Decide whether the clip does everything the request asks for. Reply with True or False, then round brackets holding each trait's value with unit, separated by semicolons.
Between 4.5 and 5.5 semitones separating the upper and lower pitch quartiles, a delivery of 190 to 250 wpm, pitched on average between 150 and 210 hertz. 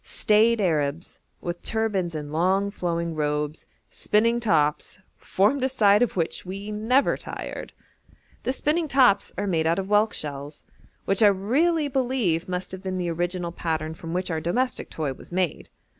False (5.2 semitones; 165 wpm; 185 Hz)